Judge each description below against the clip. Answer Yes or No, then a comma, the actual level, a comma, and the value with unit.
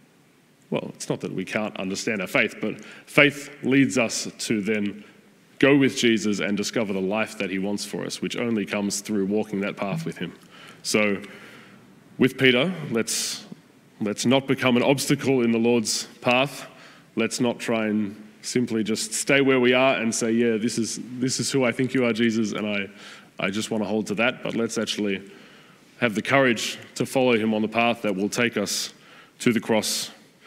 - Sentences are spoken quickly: No, average, 195 wpm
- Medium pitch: No, low, 115 Hz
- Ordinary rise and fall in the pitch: Yes, average, 3.2 semitones